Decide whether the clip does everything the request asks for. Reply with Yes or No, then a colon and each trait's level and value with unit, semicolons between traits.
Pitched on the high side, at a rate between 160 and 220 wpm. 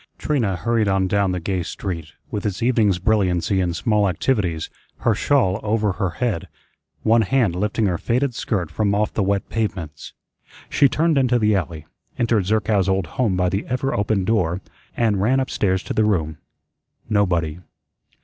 No: low, 100 Hz; average, 170 wpm